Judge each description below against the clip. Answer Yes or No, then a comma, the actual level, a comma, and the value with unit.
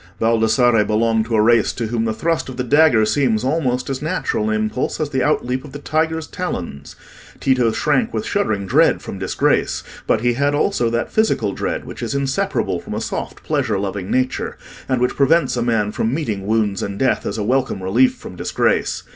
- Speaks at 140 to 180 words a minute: No, average, 200 wpm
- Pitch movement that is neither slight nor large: Yes, average, 4.4 semitones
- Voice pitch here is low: Yes, low, 120 Hz